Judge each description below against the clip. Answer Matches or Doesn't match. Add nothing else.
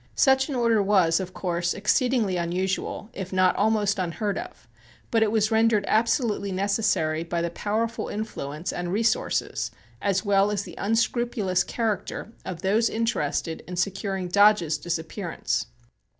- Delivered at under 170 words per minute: Matches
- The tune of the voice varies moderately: Matches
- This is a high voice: Matches